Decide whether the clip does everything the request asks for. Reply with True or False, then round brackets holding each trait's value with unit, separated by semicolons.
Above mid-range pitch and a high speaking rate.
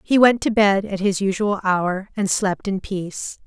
True (195 Hz; 210 wpm)